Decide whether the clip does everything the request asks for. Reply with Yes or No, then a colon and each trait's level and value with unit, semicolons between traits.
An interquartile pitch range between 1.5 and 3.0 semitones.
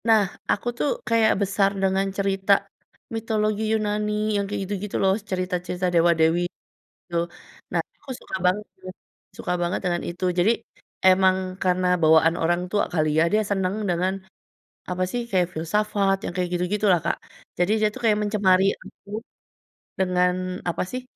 Yes: average, 2.7 semitones